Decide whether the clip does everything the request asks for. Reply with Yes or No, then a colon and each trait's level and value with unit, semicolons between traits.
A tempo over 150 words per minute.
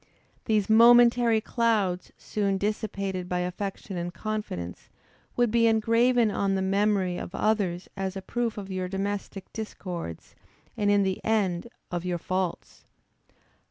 No: slow, 135 wpm